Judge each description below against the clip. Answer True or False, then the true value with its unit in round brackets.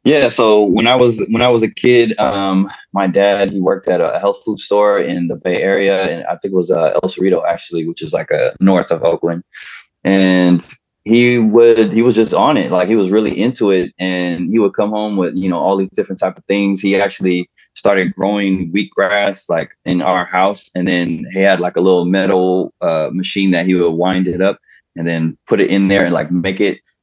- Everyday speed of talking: False (230 wpm)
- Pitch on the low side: True (95 Hz)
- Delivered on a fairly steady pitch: True (2.0 semitones)